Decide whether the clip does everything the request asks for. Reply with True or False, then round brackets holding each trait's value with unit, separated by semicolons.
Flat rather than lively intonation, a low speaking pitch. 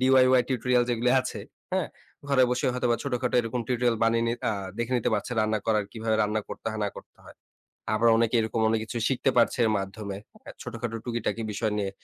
True (2.2 semitones; 115 Hz)